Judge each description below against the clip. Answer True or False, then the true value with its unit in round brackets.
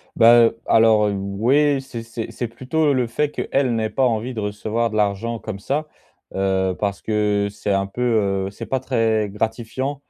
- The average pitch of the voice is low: True (115 Hz)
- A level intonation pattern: False (3.4 semitones)